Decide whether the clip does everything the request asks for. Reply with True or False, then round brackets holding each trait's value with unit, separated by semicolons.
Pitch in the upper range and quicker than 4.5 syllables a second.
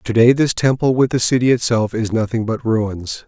False (115 Hz; 5.1 syllables/s)